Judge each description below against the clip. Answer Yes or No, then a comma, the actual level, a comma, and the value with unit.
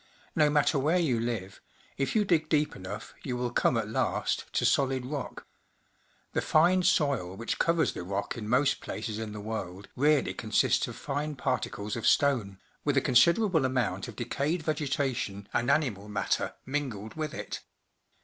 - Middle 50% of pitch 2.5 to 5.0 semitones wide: No, wide, 5.5 semitones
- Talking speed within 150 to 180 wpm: Yes, average, 170 wpm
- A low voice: Yes, low, 130 Hz